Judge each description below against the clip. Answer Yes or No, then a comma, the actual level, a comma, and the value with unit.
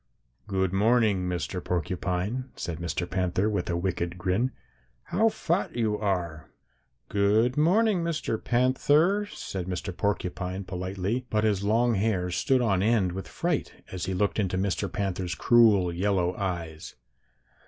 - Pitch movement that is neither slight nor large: Yes, average, 4.3 semitones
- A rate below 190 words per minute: Yes, average, 140 wpm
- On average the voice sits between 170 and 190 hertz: No, very low, 95 Hz